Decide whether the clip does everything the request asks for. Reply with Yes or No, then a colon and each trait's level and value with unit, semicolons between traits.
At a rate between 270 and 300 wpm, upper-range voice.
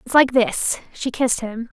No: average, 200 wpm; high, 240 Hz